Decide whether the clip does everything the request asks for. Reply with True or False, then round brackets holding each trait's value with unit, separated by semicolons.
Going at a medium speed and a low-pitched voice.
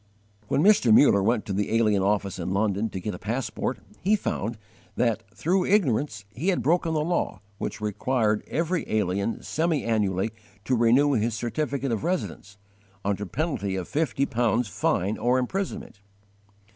True (160 wpm; 115 Hz)